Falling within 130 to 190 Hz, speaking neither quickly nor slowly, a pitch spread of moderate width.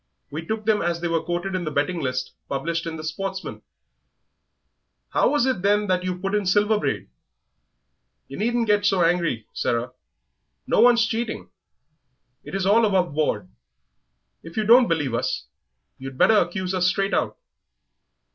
Yes: medium, 185 Hz; average, 165 wpm; average, 4.2 semitones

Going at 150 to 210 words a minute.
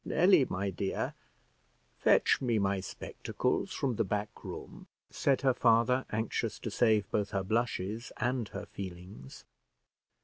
No: slow, 135 wpm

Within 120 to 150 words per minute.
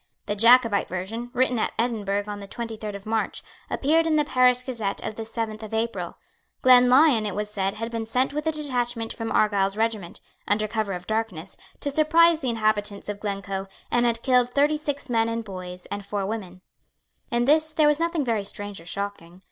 No: average, 200 wpm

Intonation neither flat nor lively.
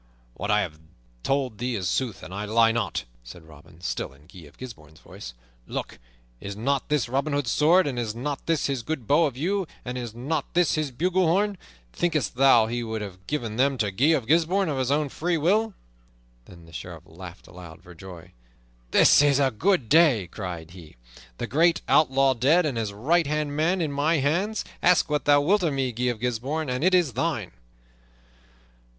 No: wide, 6.8 semitones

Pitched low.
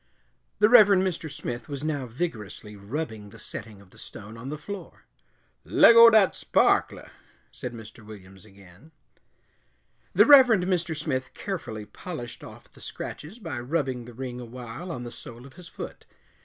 Yes: low, 130 Hz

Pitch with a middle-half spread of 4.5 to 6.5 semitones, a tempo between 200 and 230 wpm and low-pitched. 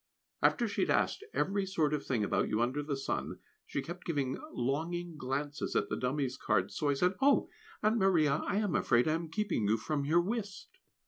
No: wide, 5.6 semitones; fast, 205 wpm; medium, 155 Hz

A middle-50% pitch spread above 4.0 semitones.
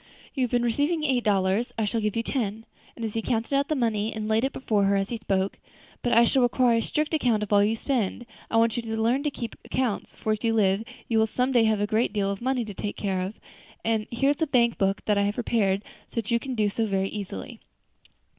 No: average, 2.9 semitones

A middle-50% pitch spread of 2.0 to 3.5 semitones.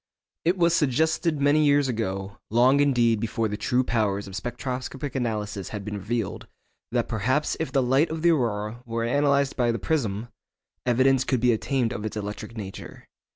No: average, 4.4 semitones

